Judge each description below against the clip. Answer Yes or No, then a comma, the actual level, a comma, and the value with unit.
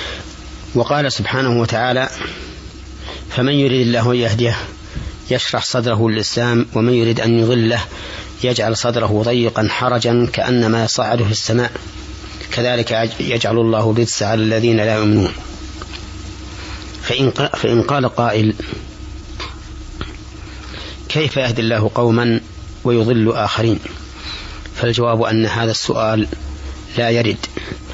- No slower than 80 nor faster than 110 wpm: Yes, average, 100 wpm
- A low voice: Yes, low, 115 Hz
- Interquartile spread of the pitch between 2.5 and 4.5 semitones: No, average, 5.2 semitones